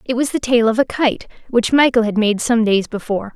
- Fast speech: Yes, fast, 250 wpm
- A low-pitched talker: No, high, 235 Hz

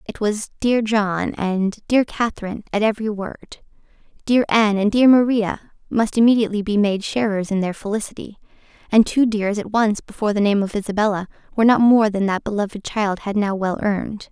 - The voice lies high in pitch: Yes, high, 210 Hz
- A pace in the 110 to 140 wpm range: No, average, 185 wpm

